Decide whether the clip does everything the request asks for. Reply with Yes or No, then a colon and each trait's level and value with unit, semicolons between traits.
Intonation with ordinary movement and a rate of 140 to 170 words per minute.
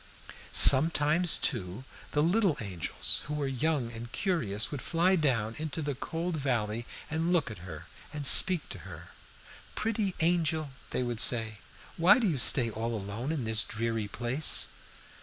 No: wide, 6.2 semitones; average, 160 wpm